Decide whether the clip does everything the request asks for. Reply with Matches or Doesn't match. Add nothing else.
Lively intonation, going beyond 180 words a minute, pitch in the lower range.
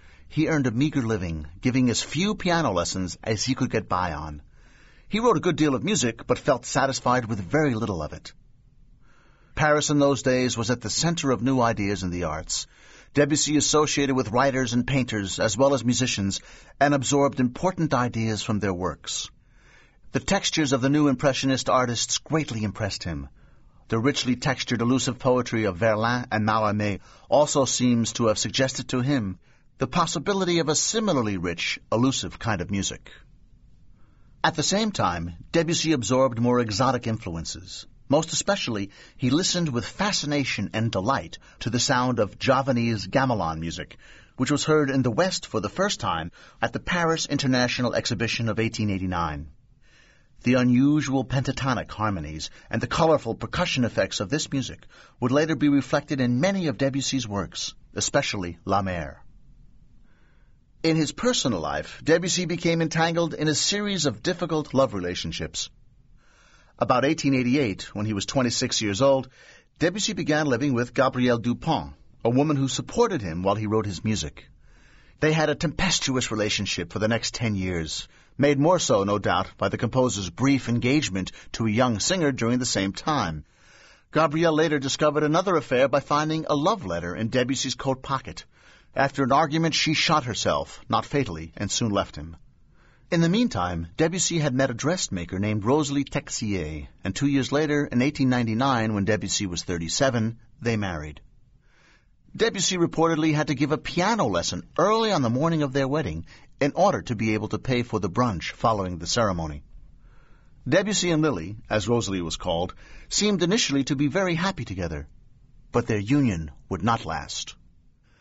Doesn't match